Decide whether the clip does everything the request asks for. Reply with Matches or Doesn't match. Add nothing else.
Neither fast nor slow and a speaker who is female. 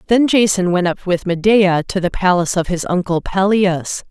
Matches